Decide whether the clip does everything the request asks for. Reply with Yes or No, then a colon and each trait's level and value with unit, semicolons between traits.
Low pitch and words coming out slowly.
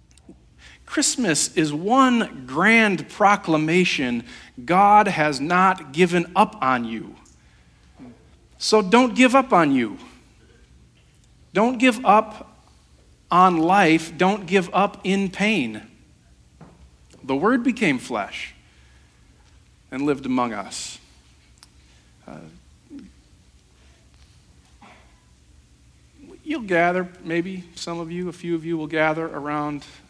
No: medium, 165 Hz; slow, 100 wpm